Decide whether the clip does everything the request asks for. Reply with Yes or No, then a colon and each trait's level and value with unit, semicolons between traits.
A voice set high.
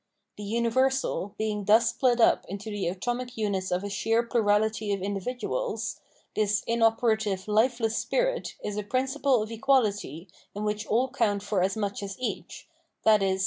Yes: high, 215 Hz